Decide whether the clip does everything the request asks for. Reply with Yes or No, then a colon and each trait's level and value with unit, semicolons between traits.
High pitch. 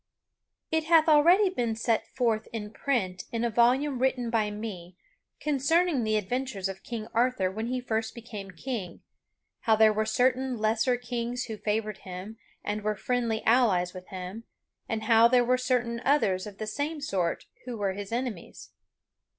Yes: high, 230 Hz